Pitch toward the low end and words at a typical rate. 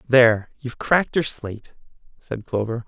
Yes: low, 125 Hz; average, 145 wpm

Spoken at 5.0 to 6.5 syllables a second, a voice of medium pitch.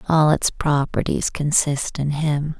No: 3.7 syllables/s; medium, 150 Hz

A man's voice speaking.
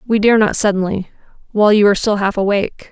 No: female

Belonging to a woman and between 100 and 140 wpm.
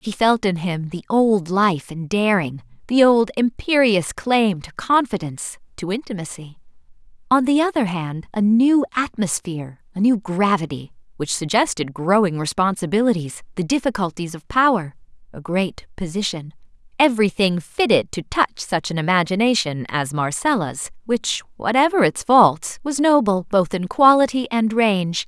Yes: female; slow, 135 wpm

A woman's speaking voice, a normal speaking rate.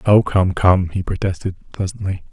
No: male; average, 155 wpm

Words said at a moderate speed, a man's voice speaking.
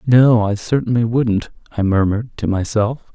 Yes: average, 155 wpm; male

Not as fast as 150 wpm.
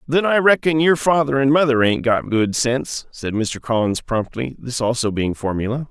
No: average, 195 wpm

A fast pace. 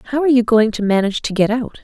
Yes: fast, 295 wpm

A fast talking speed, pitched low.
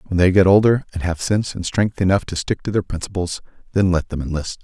Yes: fast, 245 wpm; very low, 90 Hz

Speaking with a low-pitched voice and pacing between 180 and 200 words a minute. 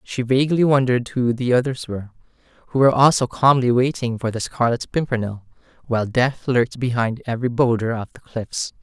No: low, 125 Hz; average, 170 wpm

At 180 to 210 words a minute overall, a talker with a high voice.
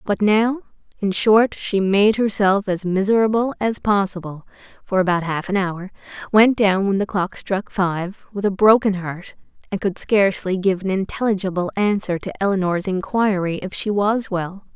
No: average, 165 wpm; high, 195 Hz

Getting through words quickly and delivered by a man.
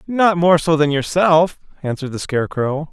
No: average, 165 wpm; male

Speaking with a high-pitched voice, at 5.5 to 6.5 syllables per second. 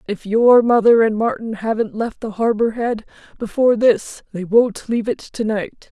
No: high, 225 Hz; 4.7 syllables/s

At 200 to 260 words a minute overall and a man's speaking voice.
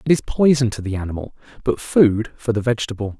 Yes: fast, 205 wpm; male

